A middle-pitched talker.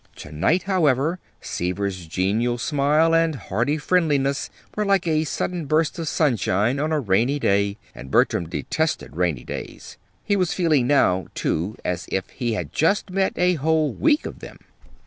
Yes: medium, 145 Hz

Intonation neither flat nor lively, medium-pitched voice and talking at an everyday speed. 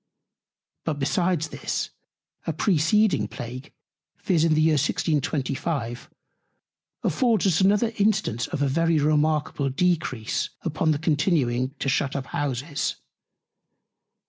No: average, 3.6 semitones; medium, 155 Hz; slow, 115 wpm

